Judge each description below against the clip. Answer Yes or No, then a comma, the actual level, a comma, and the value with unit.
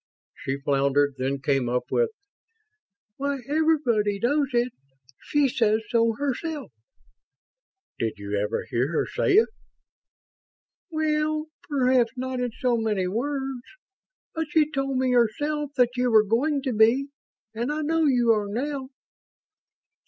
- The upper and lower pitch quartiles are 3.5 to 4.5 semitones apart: No, average, 5.3 semitones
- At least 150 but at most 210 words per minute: No, slow, 135 wpm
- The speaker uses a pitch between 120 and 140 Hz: No, very high, 250 Hz